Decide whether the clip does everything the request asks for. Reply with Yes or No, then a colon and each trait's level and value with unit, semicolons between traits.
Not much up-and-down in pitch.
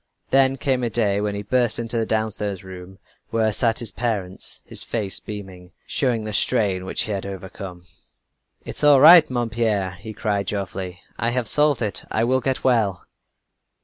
No: average, 3.7 semitones